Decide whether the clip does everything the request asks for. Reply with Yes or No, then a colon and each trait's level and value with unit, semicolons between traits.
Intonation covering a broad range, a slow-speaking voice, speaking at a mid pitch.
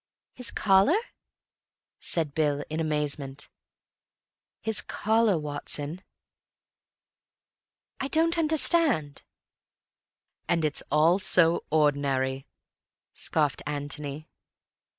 Yes: wide, 5.9 semitones; slow, 75 wpm; medium, 155 Hz